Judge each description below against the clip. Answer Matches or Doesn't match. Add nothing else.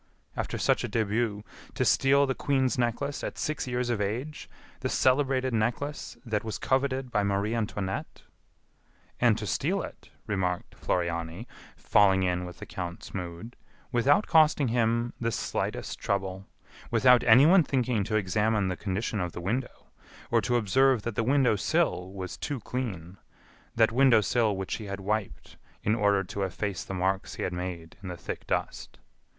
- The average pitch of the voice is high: Doesn't match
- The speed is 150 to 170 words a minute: Matches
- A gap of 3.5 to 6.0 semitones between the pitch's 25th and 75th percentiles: Matches